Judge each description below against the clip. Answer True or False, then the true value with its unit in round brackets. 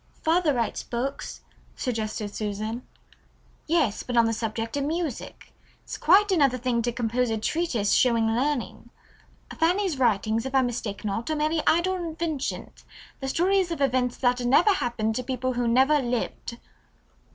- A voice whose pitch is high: True (250 Hz)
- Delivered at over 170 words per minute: False (150 wpm)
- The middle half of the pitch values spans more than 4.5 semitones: True (5.2 semitones)